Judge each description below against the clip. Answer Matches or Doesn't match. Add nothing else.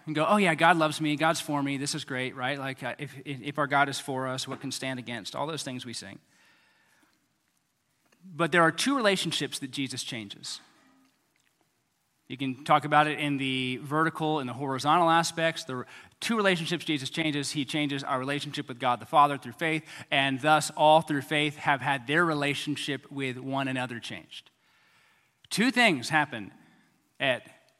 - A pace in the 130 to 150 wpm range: Doesn't match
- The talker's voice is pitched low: Doesn't match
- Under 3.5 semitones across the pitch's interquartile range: Matches